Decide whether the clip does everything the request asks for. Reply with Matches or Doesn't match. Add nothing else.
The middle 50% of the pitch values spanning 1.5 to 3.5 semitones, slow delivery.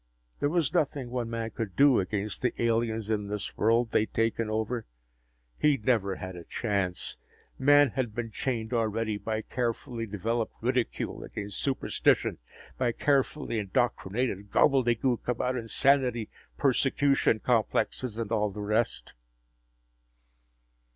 Matches